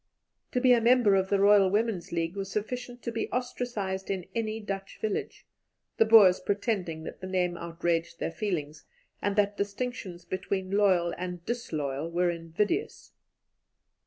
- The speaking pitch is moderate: No, high, 195 Hz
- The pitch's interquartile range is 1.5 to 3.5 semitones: No, average, 4.0 semitones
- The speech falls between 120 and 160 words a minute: Yes, average, 155 wpm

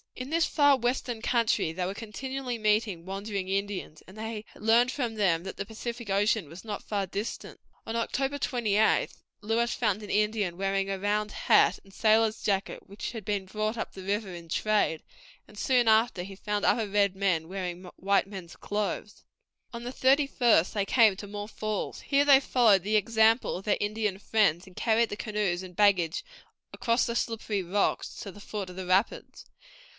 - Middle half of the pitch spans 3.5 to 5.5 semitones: No, average, 2.7 semitones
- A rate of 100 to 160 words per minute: No, average, 185 wpm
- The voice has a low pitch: No, high, 210 Hz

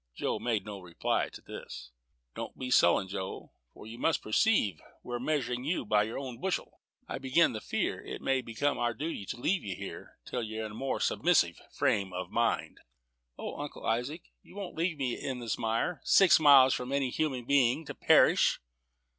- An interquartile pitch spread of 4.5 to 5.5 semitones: Yes, average, 4.8 semitones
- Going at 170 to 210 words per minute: Yes, average, 190 wpm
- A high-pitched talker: No, low, 125 Hz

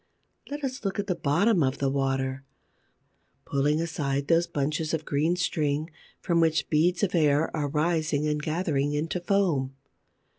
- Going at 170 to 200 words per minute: No, average, 155 wpm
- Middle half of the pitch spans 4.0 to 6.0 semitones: No, average, 3.3 semitones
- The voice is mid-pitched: Yes, medium, 155 Hz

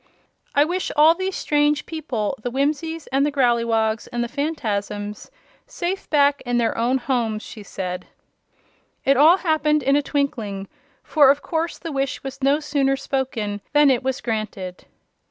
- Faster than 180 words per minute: No, average, 160 wpm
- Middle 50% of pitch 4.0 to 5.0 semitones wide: Yes, average, 4.4 semitones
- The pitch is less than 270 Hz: No, very high, 275 Hz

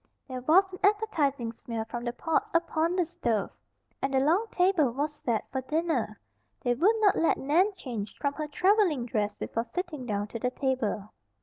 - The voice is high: Yes, very high, 280 Hz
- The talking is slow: No, average, 185 wpm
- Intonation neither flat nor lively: No, wide, 6.5 semitones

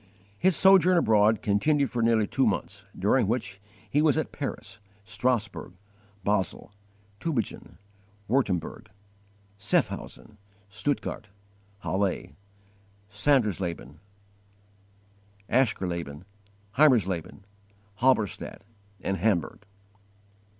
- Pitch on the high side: No, low, 110 Hz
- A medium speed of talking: No, slow, 80 wpm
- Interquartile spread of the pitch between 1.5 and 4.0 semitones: No, wide, 5.4 semitones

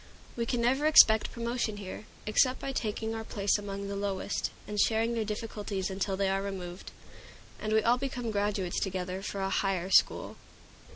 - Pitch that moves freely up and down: No, average, 2.8 semitones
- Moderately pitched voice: No, high, 210 Hz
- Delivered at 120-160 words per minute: No, average, 175 wpm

